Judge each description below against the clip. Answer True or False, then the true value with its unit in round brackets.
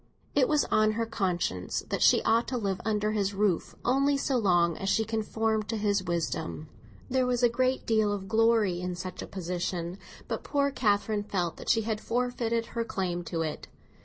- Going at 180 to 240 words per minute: True (190 wpm)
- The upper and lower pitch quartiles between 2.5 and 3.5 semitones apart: False (4.0 semitones)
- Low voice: False (210 Hz)